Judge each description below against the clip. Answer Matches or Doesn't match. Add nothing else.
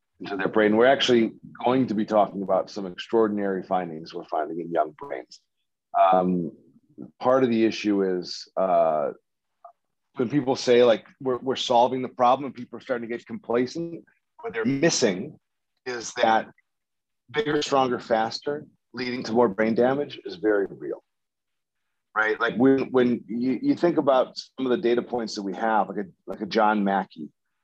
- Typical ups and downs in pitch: Matches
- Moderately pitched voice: Doesn't match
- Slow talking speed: Doesn't match